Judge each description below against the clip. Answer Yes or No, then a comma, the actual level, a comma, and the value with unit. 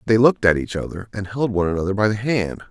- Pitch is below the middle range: Yes, low, 105 Hz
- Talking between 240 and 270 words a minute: Yes, fast, 265 wpm